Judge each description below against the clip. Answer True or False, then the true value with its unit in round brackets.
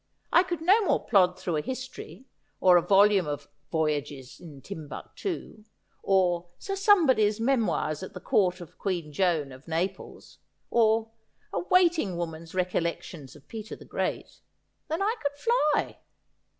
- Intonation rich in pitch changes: True (8.1 semitones)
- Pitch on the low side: False (190 Hz)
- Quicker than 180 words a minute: False (155 wpm)